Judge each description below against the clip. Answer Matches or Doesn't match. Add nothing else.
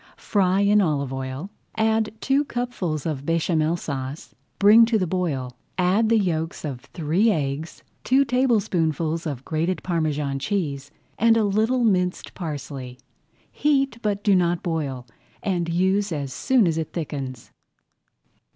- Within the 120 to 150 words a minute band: Matches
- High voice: Doesn't match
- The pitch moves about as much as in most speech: Doesn't match